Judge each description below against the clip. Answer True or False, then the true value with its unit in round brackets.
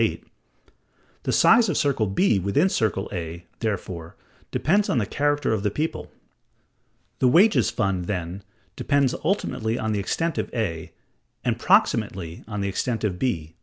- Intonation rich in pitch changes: True (7.3 semitones)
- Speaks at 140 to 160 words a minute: True (155 wpm)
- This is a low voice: True (110 Hz)